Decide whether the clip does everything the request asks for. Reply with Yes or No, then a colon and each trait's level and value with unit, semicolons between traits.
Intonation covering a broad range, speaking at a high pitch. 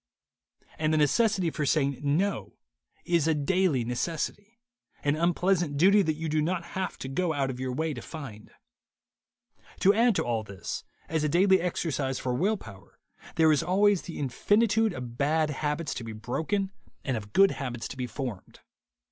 No: wide, 5.7 semitones; medium, 155 Hz